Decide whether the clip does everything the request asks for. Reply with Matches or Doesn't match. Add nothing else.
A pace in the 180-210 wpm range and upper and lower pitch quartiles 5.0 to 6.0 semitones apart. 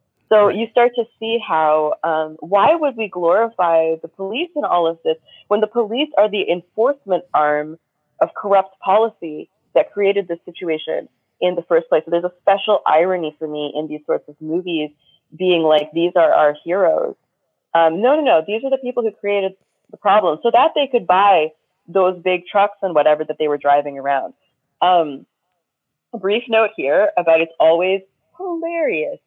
Matches